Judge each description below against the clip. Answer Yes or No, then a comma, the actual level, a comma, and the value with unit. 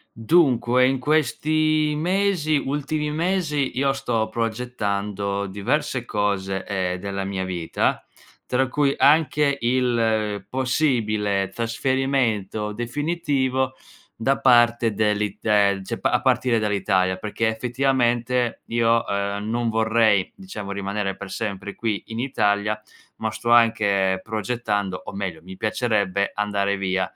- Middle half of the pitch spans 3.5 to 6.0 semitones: Yes, average, 4.6 semitones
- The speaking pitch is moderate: No, low, 115 Hz